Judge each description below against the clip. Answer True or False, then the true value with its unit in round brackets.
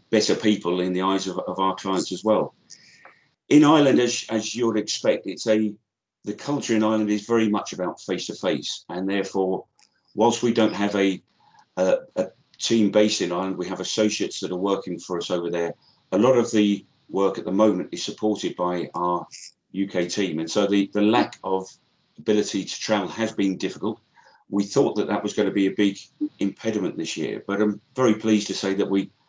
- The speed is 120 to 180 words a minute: False (205 wpm)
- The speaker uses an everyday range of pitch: False (2.3 semitones)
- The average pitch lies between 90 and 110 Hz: True (100 Hz)